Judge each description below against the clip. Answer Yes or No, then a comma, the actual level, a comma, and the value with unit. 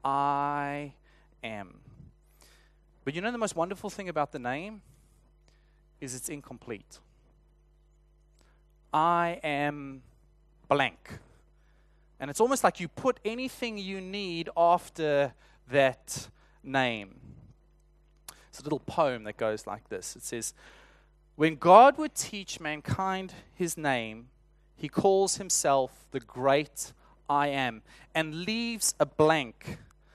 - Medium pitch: Yes, medium, 155 Hz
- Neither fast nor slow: No, slow, 115 wpm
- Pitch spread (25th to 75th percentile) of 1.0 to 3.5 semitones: No, average, 4.5 semitones